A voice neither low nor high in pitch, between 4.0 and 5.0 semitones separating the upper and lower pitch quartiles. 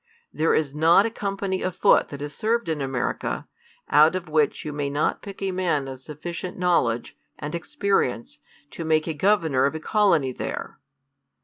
Yes: medium, 160 Hz; average, 4.4 semitones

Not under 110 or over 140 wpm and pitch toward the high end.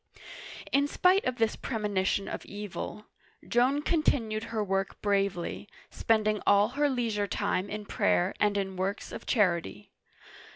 Yes: slow, 135 wpm; high, 210 Hz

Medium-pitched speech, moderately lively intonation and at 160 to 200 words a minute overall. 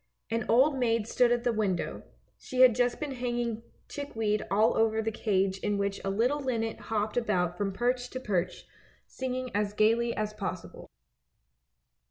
No: high, 225 Hz; average, 3.0 semitones; average, 165 wpm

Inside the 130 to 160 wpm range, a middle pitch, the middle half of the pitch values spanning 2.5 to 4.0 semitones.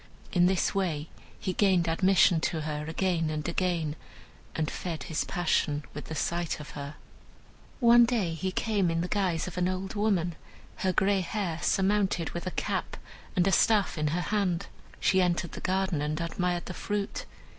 No: average, 175 wpm; medium, 180 Hz; average, 2.9 semitones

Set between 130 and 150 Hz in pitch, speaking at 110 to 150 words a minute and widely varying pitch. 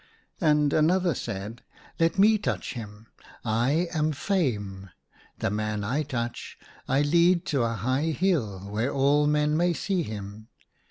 Yes: medium, 140 Hz; average, 145 wpm; wide, 7.0 semitones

